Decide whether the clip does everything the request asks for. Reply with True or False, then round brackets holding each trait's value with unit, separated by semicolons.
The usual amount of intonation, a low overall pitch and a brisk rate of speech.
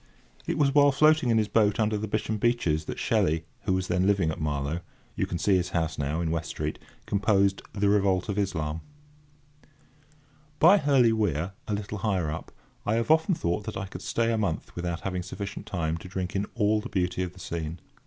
True (4.2 semitones; 95 Hz; 210 wpm)